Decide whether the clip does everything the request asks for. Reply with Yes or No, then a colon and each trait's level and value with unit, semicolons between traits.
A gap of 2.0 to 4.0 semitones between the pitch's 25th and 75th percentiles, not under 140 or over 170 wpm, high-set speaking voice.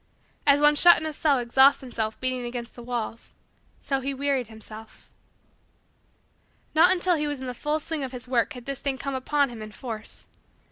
No: average, 3.3 semitones; average, 195 wpm; very high, 265 Hz